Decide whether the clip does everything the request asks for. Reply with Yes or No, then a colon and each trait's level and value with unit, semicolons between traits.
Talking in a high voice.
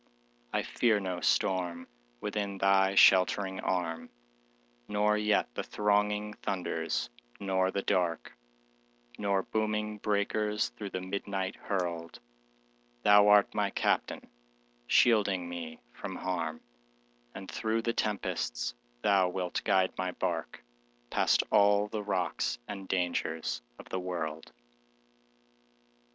No: very low, 95 Hz